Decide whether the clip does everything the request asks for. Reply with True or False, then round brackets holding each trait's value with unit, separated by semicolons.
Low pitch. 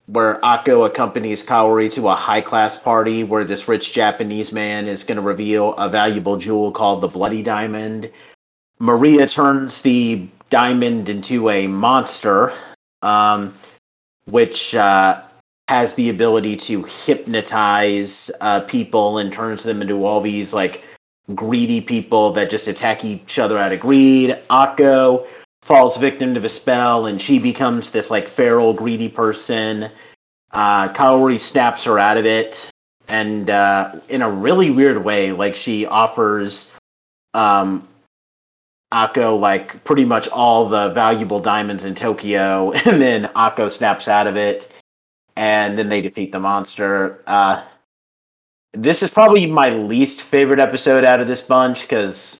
True (110 Hz)